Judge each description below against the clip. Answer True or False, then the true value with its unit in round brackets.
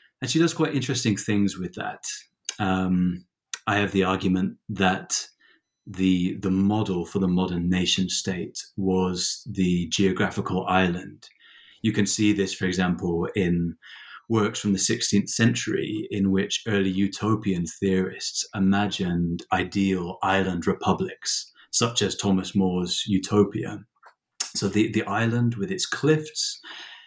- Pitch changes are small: True (2.3 semitones)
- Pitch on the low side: True (95 Hz)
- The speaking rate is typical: False (130 wpm)